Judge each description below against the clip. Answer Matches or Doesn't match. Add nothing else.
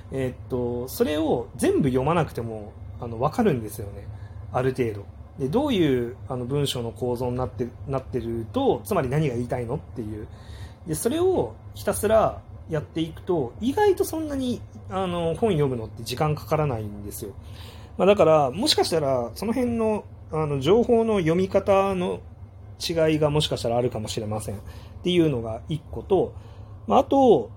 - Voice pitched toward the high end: Doesn't match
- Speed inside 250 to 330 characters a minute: Doesn't match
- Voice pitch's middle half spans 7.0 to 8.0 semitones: Matches